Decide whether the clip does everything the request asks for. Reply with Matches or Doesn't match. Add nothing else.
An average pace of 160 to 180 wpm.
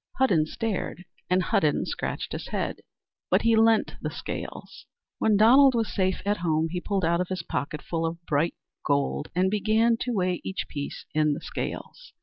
Matches